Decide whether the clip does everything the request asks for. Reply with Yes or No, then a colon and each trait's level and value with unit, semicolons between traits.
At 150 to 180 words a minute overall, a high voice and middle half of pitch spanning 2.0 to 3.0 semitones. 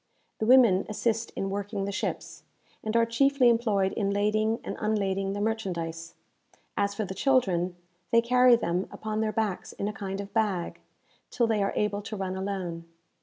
Yes: average, 175 wpm; high, 205 Hz; narrow, 2.5 semitones